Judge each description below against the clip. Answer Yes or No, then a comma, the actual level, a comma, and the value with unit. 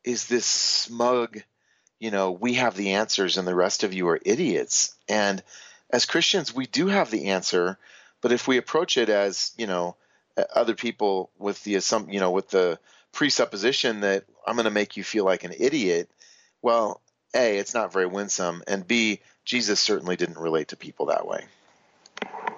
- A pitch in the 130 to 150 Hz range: No, low, 100 Hz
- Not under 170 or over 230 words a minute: Yes, average, 180 wpm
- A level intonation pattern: No, average, 3.8 semitones